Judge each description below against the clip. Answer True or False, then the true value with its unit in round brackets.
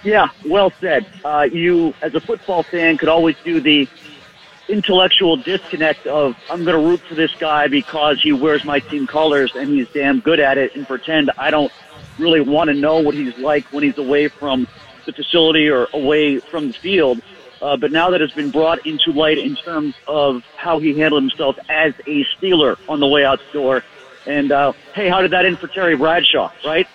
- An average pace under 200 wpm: False (205 wpm)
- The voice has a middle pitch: True (155 Hz)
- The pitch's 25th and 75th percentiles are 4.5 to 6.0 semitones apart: False (2.9 semitones)